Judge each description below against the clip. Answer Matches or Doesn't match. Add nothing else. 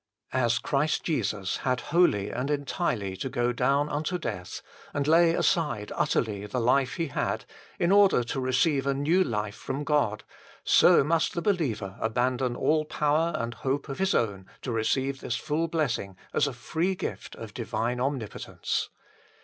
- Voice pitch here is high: Doesn't match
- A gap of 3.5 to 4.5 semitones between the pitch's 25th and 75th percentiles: Doesn't match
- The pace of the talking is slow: Doesn't match